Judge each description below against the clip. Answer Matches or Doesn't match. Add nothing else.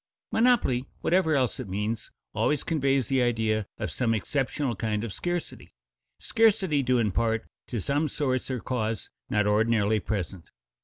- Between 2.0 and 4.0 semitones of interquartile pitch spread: Doesn't match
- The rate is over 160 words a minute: Doesn't match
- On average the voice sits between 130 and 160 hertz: Doesn't match